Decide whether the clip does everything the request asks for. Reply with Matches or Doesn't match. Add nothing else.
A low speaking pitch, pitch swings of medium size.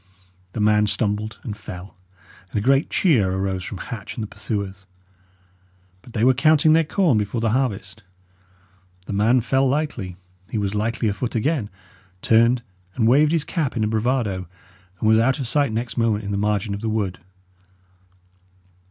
Matches